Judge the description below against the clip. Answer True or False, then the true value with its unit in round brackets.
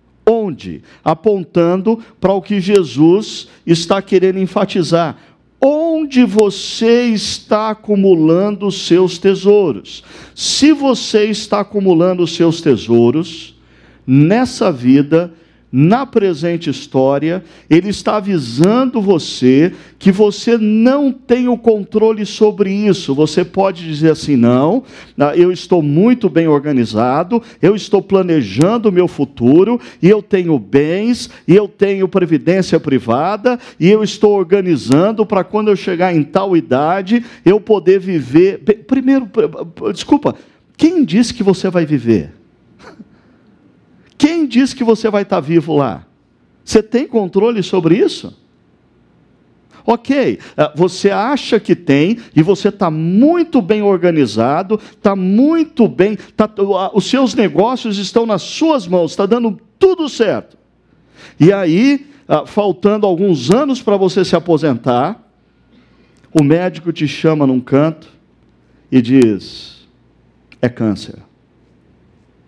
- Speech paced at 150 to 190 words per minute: False (120 wpm)